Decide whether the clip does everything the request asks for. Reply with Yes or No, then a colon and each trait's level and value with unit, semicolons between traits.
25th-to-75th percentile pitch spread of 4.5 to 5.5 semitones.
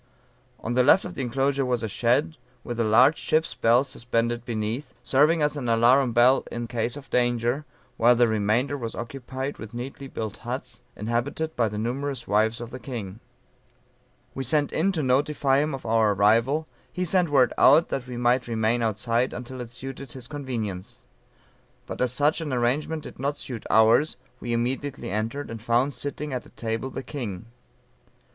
No: average, 3.3 semitones